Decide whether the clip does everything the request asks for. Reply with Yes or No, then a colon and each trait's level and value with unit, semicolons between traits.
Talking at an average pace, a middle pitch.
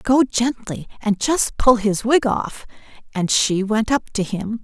No: average, 180 wpm; high, 225 Hz